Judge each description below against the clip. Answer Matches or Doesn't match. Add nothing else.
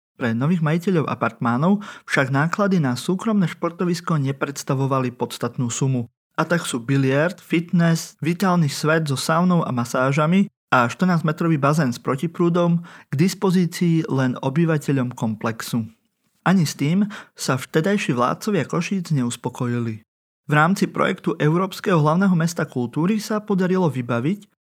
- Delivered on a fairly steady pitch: Doesn't match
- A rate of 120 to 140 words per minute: Matches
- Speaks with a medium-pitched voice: Matches